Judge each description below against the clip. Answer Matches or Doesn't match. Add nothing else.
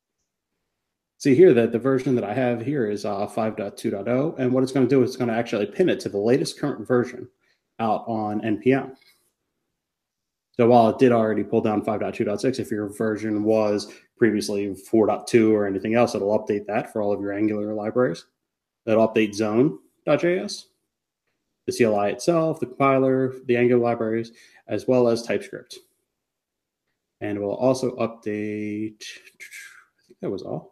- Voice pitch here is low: Matches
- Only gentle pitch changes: Doesn't match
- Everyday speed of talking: Matches